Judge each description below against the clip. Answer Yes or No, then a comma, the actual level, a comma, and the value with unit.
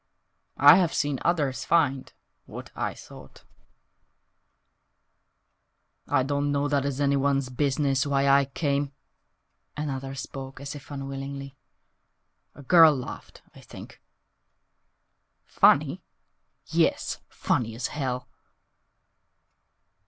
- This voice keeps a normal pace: No, slow, 100 wpm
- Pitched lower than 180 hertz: Yes, medium, 140 Hz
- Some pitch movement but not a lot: No, narrow, 1.3 semitones